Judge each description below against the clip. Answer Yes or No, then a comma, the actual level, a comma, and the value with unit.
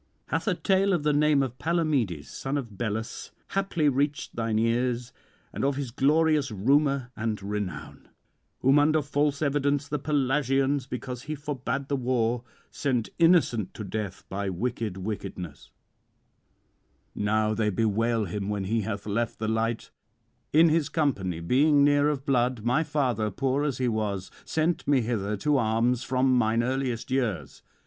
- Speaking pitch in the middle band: No, low, 125 Hz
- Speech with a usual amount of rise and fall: Yes, average, 4.7 semitones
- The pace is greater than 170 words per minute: No, average, 155 wpm